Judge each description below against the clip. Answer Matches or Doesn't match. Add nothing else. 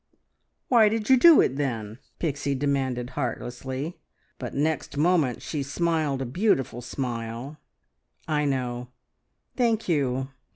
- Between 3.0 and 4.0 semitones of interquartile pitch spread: Doesn't match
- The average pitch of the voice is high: Doesn't match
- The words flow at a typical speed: Doesn't match